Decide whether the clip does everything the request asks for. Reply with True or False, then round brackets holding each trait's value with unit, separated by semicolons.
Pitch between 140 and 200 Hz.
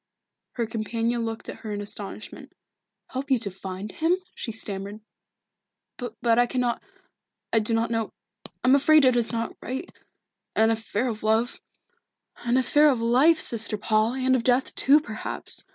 False (230 Hz)